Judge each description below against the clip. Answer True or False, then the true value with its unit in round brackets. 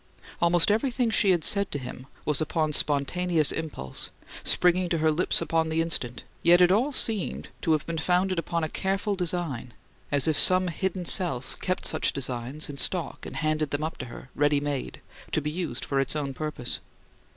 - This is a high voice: False (160 Hz)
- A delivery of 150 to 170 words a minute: False (190 wpm)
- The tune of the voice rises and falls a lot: False (3.8 semitones)